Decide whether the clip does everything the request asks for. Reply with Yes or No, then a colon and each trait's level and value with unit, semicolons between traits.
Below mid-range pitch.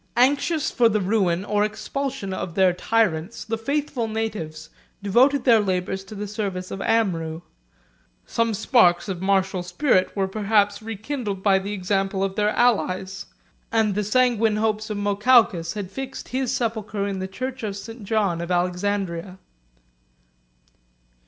No: high, 205 Hz